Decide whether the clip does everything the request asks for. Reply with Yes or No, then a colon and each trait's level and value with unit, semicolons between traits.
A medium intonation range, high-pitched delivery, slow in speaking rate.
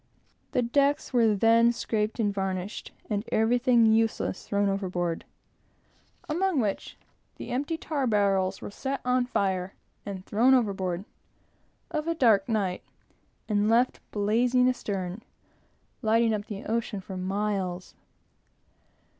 Yes: average, 4.0 semitones; high, 215 Hz; slow, 120 wpm